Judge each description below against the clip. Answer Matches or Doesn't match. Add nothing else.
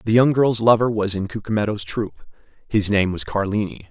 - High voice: Doesn't match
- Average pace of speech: Matches